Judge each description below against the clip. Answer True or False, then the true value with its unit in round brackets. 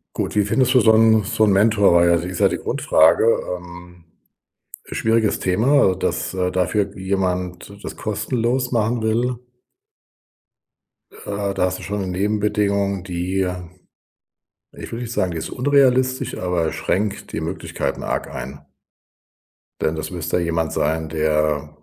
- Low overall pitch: True (95 Hz)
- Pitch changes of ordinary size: True (4.0 semitones)